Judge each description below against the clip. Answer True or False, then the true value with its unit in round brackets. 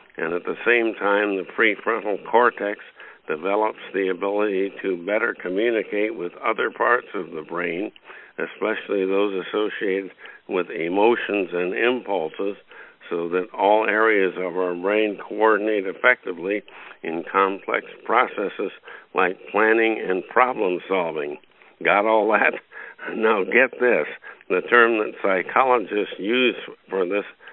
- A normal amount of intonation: False (2.3 semitones)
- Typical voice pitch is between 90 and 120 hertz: True (100 Hz)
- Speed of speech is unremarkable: False (125 wpm)